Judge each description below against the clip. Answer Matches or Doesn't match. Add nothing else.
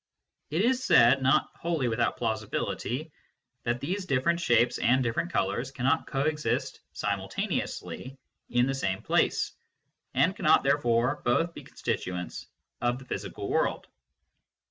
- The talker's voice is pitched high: Doesn't match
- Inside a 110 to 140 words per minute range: Matches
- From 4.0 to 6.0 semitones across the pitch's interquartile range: Matches